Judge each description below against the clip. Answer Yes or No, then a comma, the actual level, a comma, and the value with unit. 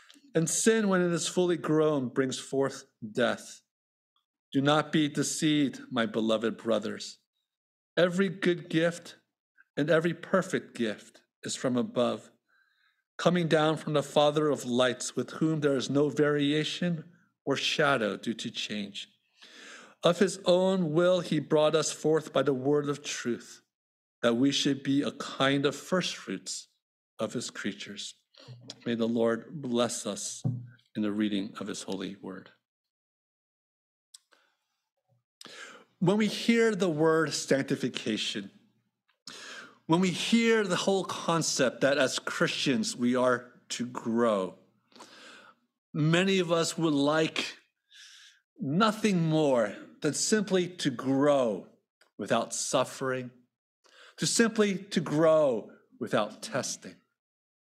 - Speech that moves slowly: Yes, slow, 125 wpm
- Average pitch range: No, wide, 5.8 semitones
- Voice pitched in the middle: Yes, medium, 155 Hz